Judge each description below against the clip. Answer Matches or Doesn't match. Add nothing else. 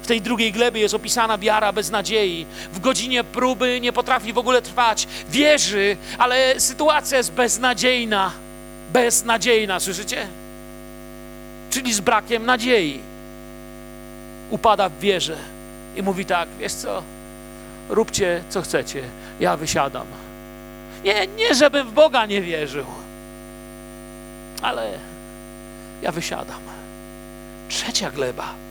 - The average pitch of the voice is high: Matches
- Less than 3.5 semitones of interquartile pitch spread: Doesn't match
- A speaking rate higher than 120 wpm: Doesn't match